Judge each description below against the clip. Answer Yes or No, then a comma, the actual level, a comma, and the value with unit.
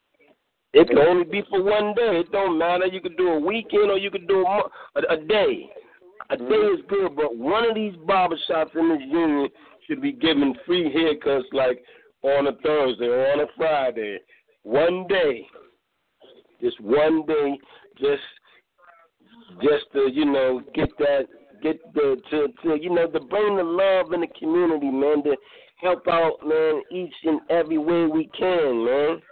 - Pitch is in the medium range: Yes, medium, 180 Hz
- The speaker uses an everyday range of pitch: No, wide, 6.6 semitones